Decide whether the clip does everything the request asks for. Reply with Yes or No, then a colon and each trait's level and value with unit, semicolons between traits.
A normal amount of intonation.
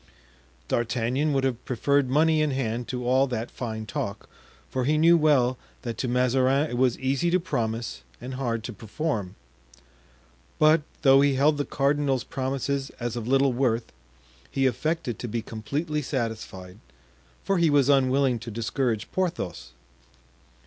Yes: average, 3.4 semitones